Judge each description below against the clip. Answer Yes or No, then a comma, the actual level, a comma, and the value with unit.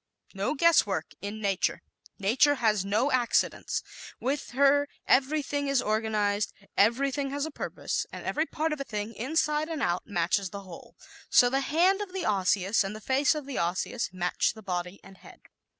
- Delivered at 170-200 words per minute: Yes, average, 180 wpm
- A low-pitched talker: No, high, 235 Hz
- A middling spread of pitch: No, wide, 6.2 semitones